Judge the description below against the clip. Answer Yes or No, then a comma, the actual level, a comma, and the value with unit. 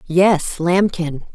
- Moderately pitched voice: Yes, medium, 175 Hz